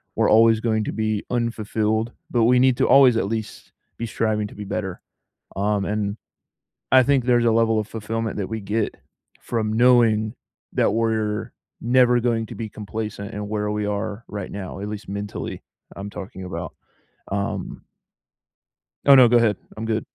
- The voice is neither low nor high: No, low, 110 Hz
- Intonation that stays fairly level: Yes, narrow, 1.9 semitones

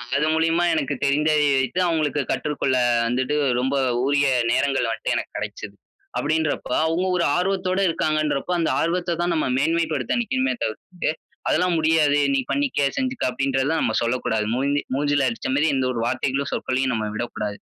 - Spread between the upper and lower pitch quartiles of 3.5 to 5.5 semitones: Yes, average, 4.1 semitones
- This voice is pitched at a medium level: Yes, medium, 145 Hz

